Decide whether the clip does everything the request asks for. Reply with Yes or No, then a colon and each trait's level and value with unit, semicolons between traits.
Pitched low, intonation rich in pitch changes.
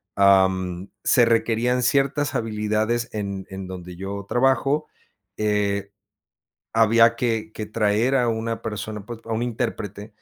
No: low, 110 Hz; average, 2.8 semitones